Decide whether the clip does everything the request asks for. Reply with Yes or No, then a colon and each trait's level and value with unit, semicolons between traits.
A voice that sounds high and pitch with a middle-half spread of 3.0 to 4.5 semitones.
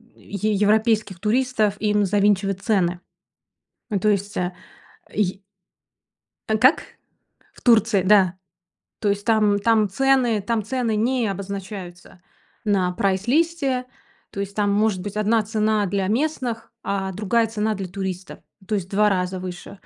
No: high, 205 Hz; narrow, 2.4 semitones